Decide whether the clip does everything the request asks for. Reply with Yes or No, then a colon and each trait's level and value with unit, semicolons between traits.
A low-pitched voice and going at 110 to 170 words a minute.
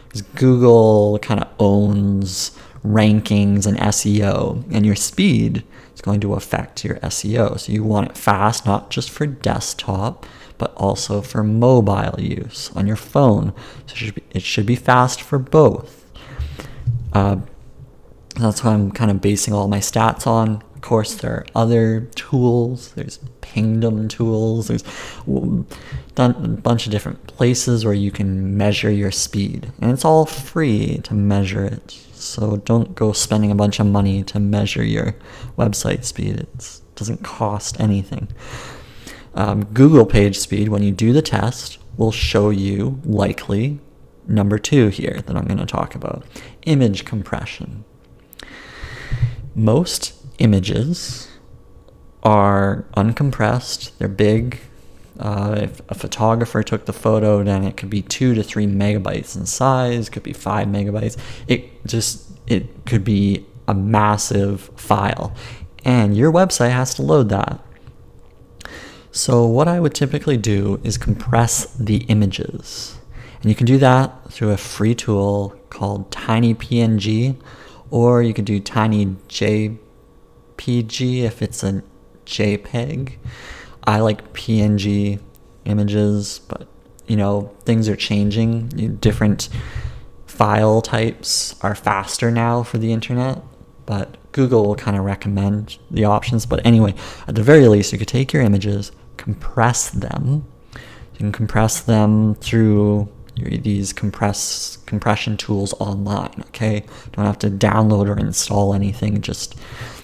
Yes: low, 110 Hz; average, 140 wpm